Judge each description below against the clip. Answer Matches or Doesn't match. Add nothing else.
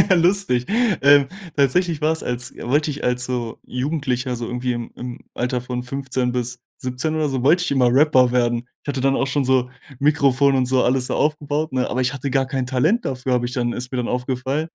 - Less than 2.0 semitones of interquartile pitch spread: Doesn't match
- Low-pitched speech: Matches